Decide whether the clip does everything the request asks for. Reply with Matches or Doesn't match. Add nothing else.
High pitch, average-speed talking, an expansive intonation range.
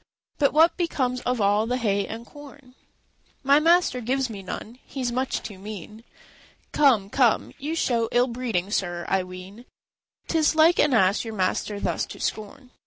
Doesn't match